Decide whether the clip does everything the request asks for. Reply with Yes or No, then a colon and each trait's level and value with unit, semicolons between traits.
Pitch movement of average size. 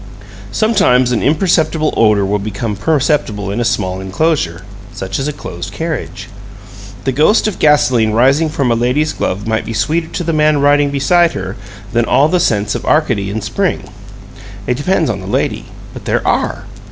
No: wide, 6.8 semitones